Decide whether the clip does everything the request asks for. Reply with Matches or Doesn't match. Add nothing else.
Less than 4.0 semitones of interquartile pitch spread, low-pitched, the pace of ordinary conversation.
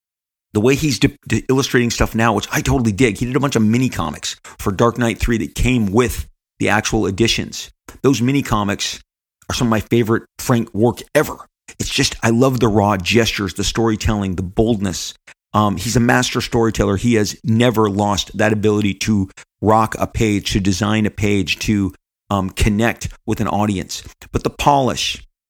Matches